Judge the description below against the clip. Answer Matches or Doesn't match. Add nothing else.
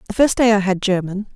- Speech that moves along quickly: Matches